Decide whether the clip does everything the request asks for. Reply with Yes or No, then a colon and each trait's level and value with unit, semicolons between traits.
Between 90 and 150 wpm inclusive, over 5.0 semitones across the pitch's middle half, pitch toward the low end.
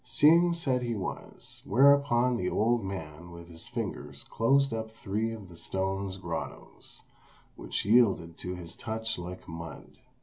Yes: average, 145 wpm; wide, 5.5 semitones; low, 100 Hz